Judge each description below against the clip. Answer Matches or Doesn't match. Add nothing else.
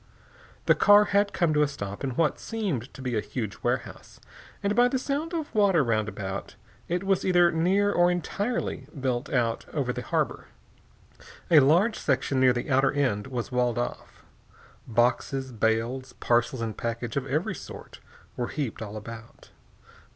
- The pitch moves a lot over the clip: Matches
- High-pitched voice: Doesn't match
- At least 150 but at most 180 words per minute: Matches